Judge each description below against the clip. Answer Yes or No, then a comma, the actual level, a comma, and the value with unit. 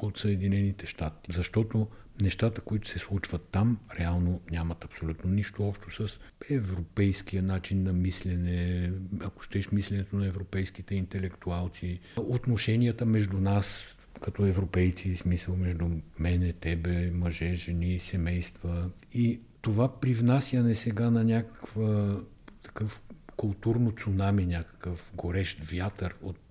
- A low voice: Yes, very low, 95 Hz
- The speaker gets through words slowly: Yes, slow, 110 wpm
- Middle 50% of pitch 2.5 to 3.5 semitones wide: Yes, average, 3.2 semitones